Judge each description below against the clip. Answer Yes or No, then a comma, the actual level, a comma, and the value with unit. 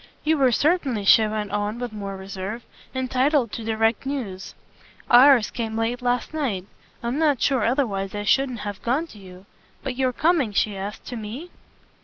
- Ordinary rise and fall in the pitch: Yes, average, 4.4 semitones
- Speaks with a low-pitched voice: No, high, 235 Hz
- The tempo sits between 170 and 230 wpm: Yes, average, 175 wpm